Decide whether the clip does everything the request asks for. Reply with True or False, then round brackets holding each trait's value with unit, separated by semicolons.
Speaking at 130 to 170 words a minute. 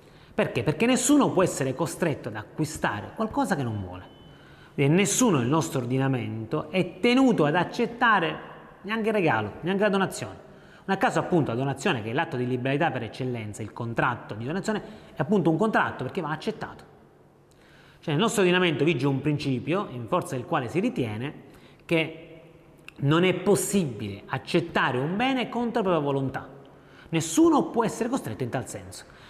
True (165 wpm)